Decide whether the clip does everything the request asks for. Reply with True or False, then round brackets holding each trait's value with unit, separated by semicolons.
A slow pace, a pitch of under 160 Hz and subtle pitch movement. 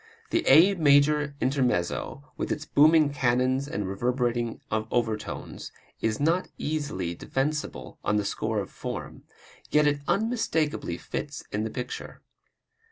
False (125 wpm; 135 Hz; 5.1 semitones)